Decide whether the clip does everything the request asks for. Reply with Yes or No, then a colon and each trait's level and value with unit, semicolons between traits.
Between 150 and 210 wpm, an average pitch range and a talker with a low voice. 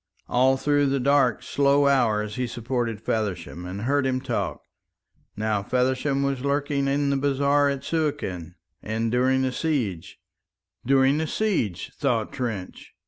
No: average, 140 wpm; average, 4.0 semitones; low, 130 Hz